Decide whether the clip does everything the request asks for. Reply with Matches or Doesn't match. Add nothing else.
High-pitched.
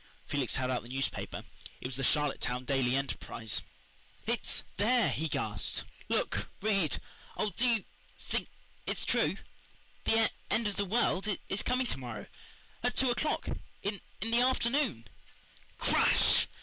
Matches